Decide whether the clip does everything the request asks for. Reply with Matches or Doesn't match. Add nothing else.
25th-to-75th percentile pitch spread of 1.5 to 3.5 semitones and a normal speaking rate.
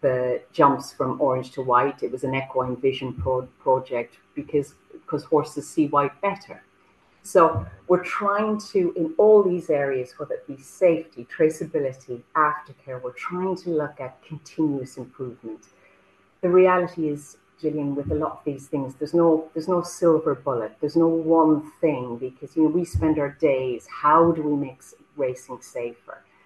Doesn't match